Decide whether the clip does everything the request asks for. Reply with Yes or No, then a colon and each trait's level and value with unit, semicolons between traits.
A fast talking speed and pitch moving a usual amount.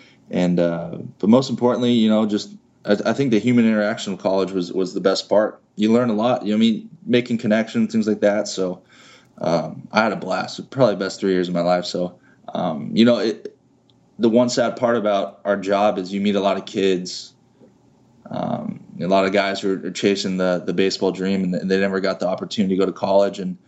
Yes: fast, 225 wpm; average, 3.1 semitones